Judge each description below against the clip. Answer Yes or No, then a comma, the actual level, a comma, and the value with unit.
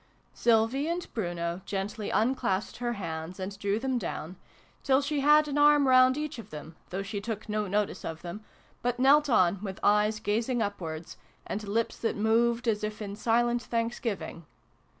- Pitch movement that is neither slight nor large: Yes, average, 3.7 semitones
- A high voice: Yes, high, 220 Hz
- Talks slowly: No, average, 170 wpm